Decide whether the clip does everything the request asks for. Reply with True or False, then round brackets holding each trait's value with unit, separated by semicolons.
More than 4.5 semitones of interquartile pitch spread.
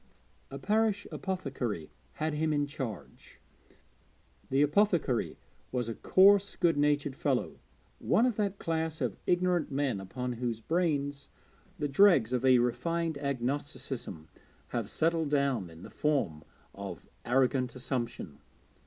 True (5.0 semitones)